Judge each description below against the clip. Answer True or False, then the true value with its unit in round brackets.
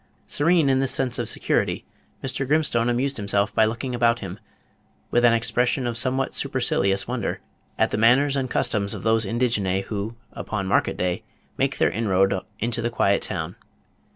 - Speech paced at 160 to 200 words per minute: True (170 wpm)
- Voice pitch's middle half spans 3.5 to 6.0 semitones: True (4.2 semitones)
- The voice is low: True (115 Hz)